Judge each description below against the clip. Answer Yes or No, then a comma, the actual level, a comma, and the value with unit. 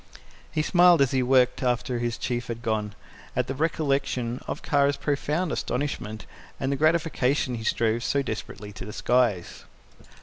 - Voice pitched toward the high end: No, low, 125 Hz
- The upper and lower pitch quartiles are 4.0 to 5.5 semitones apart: No, average, 3.4 semitones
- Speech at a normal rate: Yes, average, 155 wpm